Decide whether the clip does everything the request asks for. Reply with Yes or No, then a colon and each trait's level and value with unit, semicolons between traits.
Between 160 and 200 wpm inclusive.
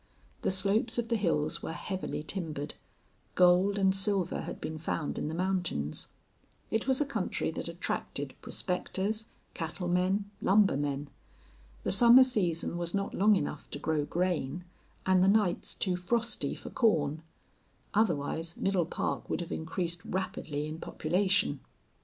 No: average, 140 wpm